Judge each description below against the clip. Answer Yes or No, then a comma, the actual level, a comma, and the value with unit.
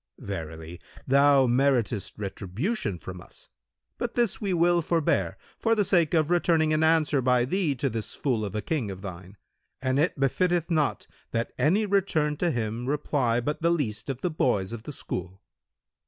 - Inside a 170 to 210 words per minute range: Yes, average, 175 wpm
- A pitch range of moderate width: No, wide, 7.5 semitones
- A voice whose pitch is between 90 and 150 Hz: Yes, medium, 140 Hz